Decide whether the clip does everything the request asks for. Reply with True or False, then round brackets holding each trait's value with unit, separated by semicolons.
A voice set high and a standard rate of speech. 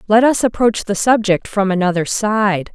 True (205 Hz; 175 wpm)